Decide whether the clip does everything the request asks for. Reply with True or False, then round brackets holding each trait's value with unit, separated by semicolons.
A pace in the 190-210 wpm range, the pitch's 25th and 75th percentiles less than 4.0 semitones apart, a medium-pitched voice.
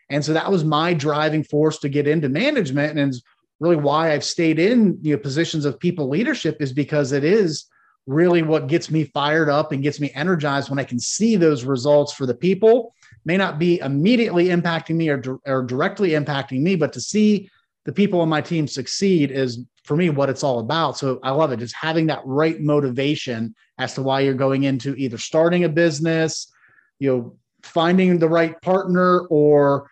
True (200 wpm; 3.5 semitones; 150 Hz)